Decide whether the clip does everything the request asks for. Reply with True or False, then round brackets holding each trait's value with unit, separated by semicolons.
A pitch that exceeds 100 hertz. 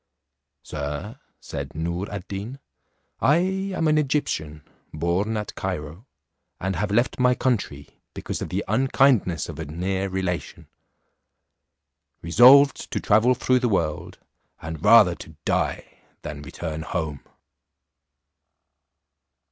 False (95 Hz)